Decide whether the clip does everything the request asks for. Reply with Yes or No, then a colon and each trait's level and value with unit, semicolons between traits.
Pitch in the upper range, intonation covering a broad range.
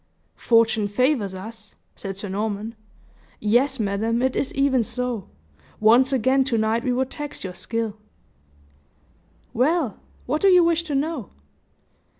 No: high, 235 Hz; average, 3.9 semitones